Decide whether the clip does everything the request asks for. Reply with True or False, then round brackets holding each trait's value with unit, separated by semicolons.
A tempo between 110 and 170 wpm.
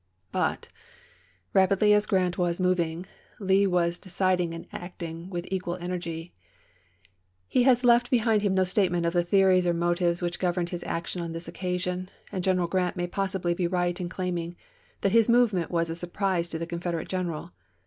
False (180 wpm)